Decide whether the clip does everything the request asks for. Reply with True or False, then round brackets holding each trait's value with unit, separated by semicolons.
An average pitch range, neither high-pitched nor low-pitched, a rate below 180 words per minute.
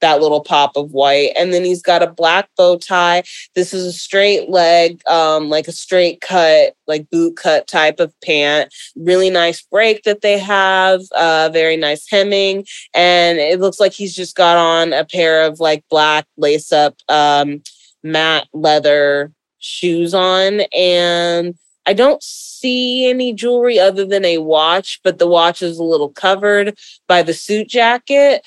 True (3.7 semitones; 175 Hz; 170 wpm)